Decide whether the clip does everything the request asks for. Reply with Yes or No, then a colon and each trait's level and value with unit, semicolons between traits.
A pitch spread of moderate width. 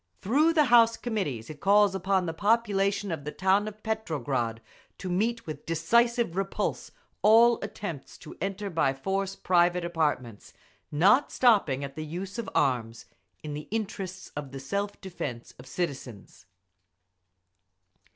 No: wide, 6.0 semitones